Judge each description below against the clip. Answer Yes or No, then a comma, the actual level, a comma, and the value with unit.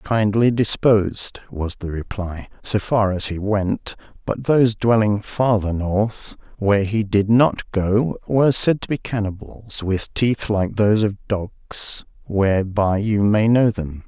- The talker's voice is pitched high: No, low, 105 Hz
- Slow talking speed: No, average, 155 wpm